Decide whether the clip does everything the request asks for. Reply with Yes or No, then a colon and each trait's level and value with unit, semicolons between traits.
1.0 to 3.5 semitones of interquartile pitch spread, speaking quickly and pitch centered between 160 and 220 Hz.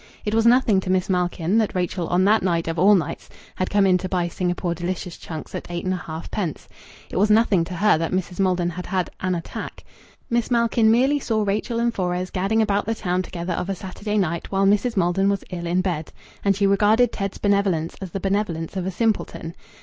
Yes: average, 2.9 semitones; fast, 215 wpm; high, 190 Hz